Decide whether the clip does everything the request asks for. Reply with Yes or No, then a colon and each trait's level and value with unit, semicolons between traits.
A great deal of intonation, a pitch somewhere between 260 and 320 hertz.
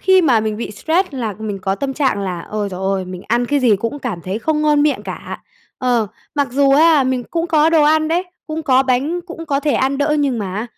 Yes: wide, 6.0 semitones; very high, 270 Hz